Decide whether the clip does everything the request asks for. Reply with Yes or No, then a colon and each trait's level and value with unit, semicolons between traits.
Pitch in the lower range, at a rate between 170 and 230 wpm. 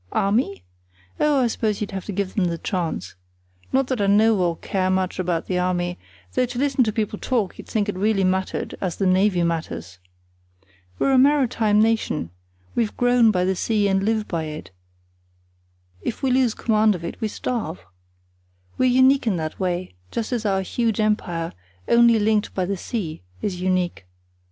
No: high, 200 Hz; average, 180 wpm